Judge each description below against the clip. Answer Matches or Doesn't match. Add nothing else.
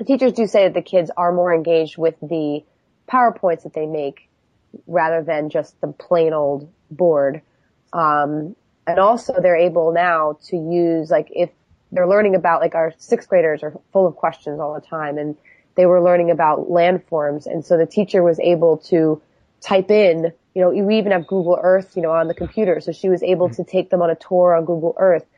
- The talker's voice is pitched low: Doesn't match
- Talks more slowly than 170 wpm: Doesn't match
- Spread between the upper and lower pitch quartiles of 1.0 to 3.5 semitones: Matches